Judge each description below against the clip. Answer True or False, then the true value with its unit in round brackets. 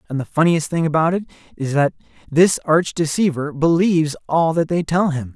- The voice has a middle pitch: True (160 Hz)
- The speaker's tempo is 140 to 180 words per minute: False (190 wpm)